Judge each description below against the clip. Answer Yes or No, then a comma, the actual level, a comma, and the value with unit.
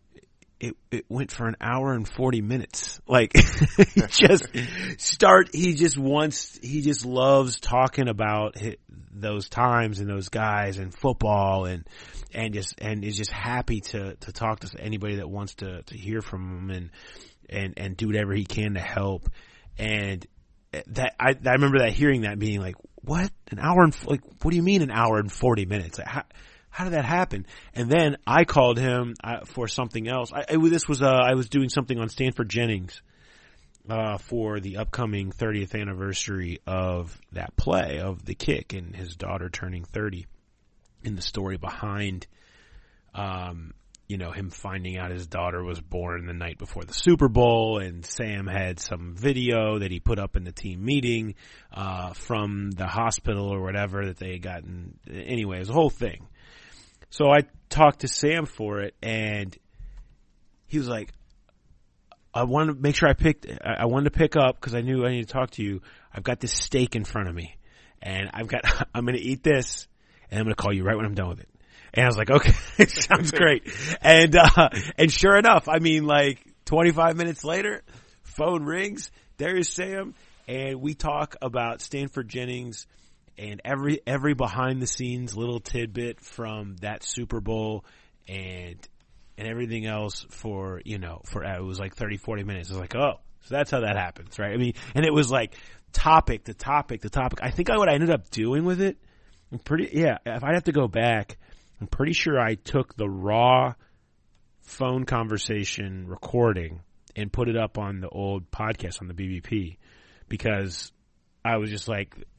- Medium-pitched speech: No, low, 110 Hz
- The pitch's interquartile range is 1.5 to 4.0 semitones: No, average, 5.0 semitones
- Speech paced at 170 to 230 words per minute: Yes, average, 190 wpm